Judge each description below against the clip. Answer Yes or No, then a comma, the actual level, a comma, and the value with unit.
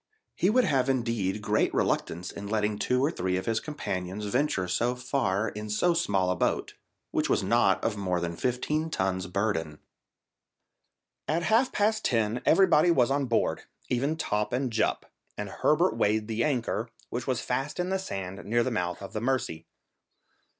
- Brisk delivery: No, average, 175 wpm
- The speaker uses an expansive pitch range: Yes, wide, 5.8 semitones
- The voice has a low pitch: Yes, low, 115 Hz